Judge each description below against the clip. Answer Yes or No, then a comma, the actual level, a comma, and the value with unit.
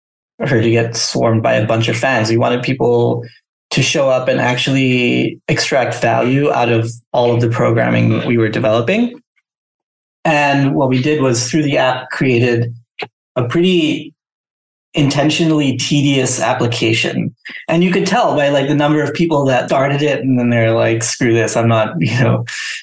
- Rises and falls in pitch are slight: No, average, 3.8 semitones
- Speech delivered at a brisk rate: No, average, 175 wpm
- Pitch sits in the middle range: No, low, 125 Hz